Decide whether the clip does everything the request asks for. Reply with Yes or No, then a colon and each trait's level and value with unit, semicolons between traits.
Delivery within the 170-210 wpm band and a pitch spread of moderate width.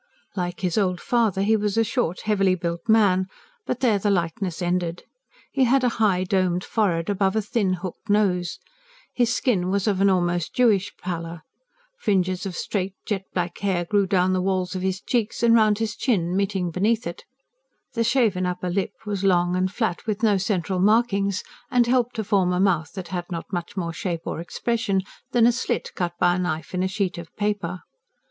Yes: average, 195 wpm; average, 3.0 semitones